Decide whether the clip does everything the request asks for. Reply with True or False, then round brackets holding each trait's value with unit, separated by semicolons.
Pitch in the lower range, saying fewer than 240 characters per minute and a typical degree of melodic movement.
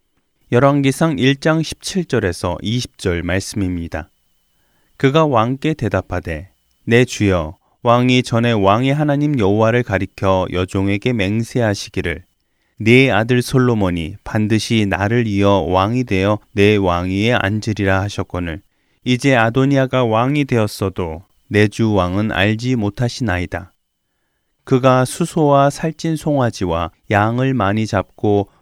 False (110 Hz; 260 characters per minute; 4.9 semitones)